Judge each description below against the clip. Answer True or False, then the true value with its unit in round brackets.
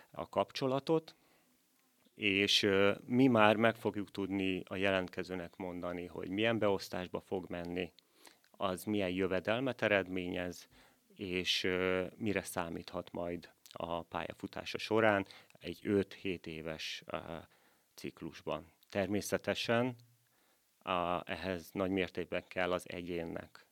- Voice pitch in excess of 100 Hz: False (95 Hz)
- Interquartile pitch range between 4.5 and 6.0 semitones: False (2.7 semitones)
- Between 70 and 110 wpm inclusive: True (105 wpm)